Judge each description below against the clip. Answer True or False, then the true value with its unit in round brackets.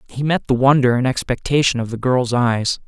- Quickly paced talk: True (210 wpm)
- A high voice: False (125 Hz)